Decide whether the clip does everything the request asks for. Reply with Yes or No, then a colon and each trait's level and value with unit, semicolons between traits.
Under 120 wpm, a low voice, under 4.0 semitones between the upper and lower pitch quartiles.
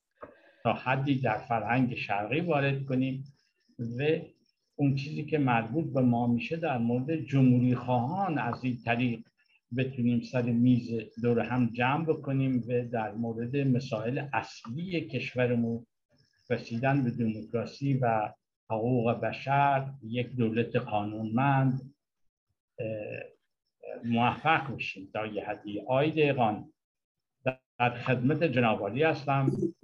Yes: average, 110 wpm; low, 125 Hz; average, 2.9 semitones